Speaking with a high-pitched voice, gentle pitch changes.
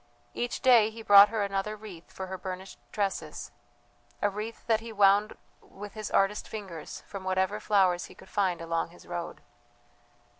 Yes: high, 200 Hz; narrow, 2.3 semitones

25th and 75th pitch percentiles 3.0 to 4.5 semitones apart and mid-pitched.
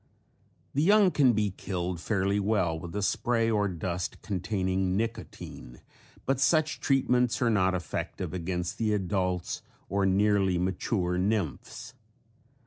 No: average, 3.7 semitones; low, 100 Hz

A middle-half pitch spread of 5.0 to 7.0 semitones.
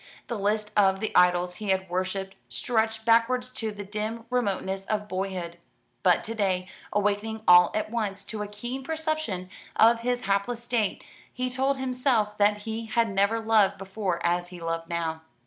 No: average, 3.2 semitones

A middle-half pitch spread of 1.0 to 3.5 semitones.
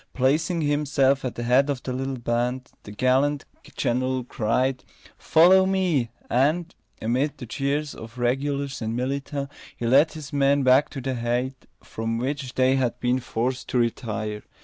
Yes: narrow, 2.6 semitones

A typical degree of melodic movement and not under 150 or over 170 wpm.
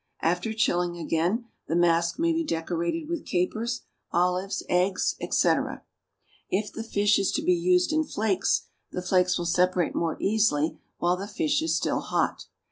Yes: average, 3.8 semitones; average, 160 wpm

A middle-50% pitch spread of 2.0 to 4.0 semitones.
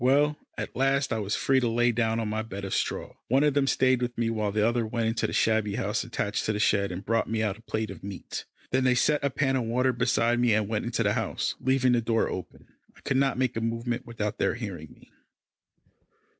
Yes: average, 2.8 semitones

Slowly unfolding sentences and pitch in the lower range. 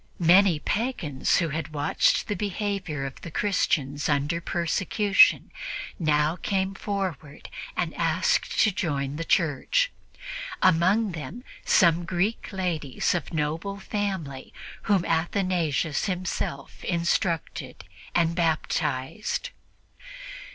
No: slow, 100 wpm; medium, 170 Hz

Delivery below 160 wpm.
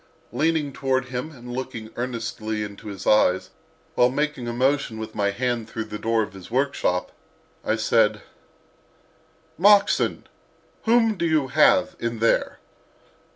Yes: slow, 135 wpm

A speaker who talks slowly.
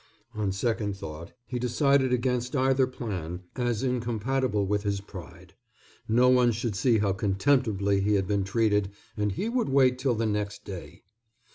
No: average, 160 wpm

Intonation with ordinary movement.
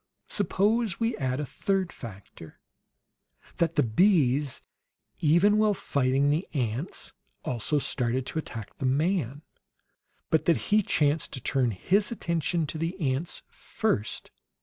No: wide, 6.2 semitones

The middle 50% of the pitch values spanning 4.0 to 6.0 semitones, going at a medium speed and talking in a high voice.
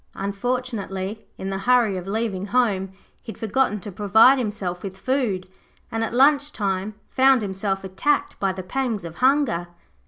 Yes: average, 4.6 semitones; average, 160 wpm; high, 210 Hz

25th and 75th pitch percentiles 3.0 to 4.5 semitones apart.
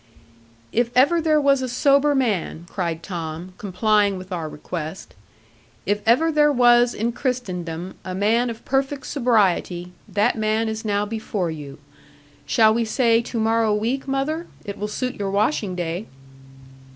No: average, 5.2 semitones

